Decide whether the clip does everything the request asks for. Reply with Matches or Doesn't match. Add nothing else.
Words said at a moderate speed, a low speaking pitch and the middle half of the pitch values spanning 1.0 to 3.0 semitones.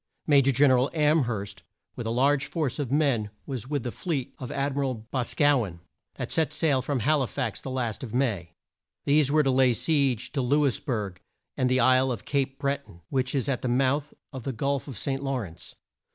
Doesn't match